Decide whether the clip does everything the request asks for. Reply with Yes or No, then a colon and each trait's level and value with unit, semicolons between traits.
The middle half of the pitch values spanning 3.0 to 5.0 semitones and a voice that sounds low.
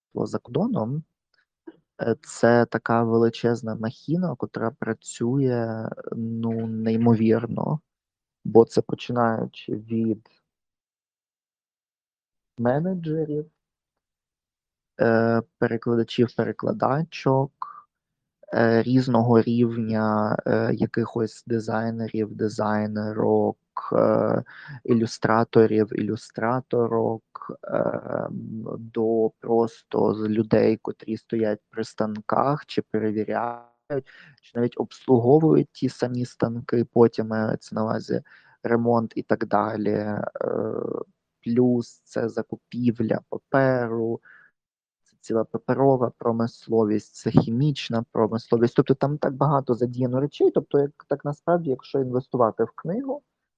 No: narrow, 2.4 semitones; low, 115 Hz